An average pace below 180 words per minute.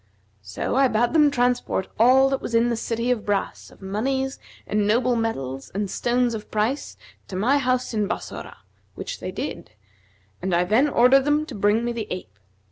No: average, 190 wpm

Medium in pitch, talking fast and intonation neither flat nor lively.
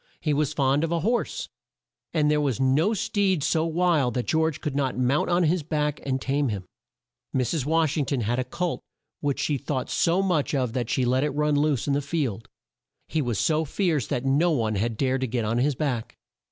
Yes: medium, 145 Hz; fast, 220 wpm; average, 3.8 semitones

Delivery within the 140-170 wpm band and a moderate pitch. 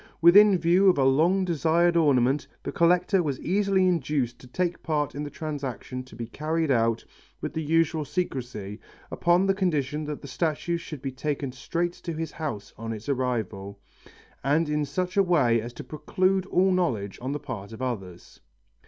No: average, 180 wpm; medium, 150 Hz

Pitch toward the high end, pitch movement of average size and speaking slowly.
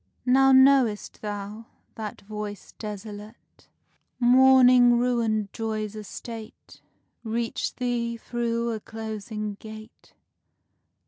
No: high, 225 Hz; narrow, 2.3 semitones; slow, 85 wpm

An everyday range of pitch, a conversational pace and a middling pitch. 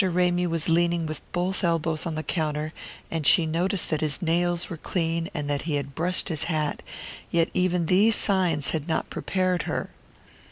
No: narrow, 2.2 semitones; average, 185 wpm; medium, 165 Hz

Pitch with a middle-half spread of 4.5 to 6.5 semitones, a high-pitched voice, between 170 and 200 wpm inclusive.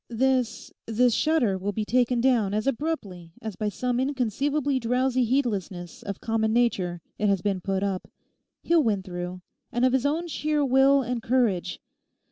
No: average, 4.9 semitones; high, 235 Hz; average, 160 wpm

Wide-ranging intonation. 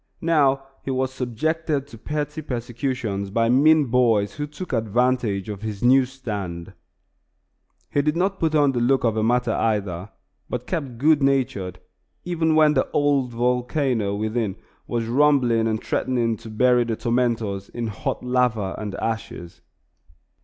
No: average, 4.1 semitones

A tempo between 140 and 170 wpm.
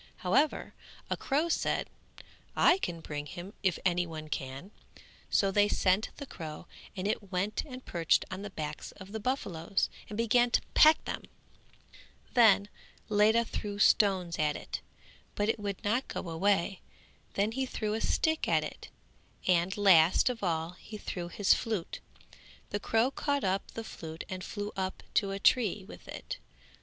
Yes: average, 165 wpm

